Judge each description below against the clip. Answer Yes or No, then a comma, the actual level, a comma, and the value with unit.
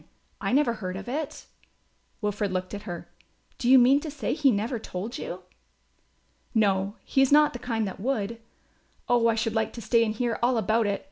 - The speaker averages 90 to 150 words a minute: No, average, 200 wpm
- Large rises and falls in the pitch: No, average, 3.8 semitones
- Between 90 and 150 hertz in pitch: No, high, 230 Hz